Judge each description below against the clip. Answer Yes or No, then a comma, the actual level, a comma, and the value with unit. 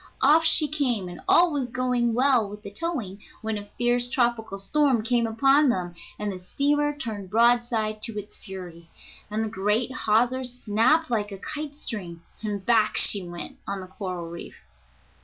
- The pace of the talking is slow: No, average, 175 wpm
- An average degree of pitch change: Yes, average, 4.2 semitones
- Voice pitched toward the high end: Yes, high, 225 Hz